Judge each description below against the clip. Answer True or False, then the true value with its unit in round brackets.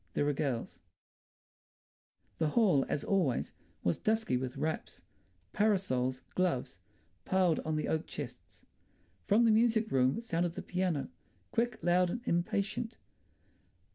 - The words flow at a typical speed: False (125 wpm)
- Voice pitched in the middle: True (175 Hz)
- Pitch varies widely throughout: True (7.3 semitones)